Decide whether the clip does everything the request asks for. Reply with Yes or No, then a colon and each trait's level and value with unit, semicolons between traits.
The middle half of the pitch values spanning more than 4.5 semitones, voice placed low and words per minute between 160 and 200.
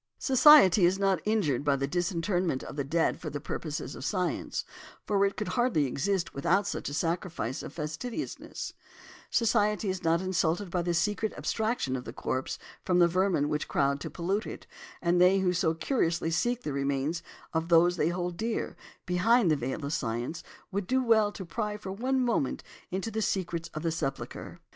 No: average, 4.9 semitones; medium, 175 Hz; average, 185 wpm